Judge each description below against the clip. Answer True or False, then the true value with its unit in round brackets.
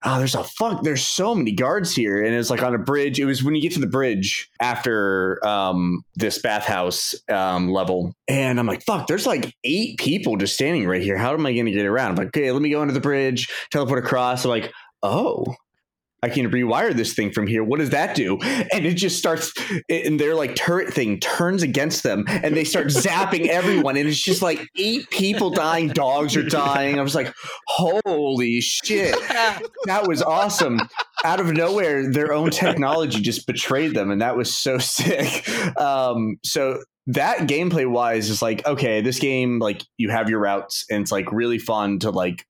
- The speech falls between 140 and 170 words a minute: False (200 wpm)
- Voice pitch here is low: True (130 Hz)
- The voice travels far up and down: True (5.7 semitones)